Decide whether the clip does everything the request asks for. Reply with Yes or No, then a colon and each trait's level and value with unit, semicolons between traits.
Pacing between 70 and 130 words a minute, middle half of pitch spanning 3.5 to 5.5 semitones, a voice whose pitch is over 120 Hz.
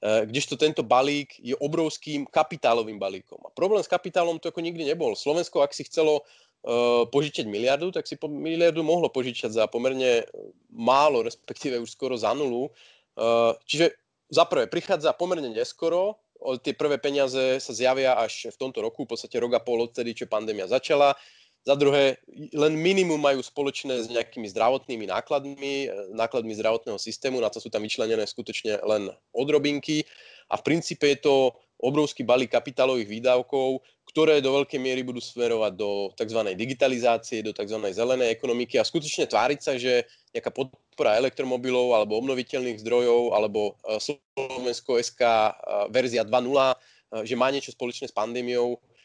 No: average, 150 wpm; average, 4.2 semitones; low, 130 Hz